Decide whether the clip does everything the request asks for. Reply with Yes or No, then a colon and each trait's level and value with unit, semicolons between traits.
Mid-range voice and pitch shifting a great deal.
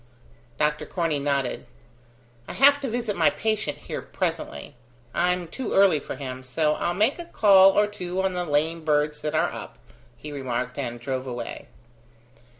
Yes: medium, 160 Hz; wide, 5.8 semitones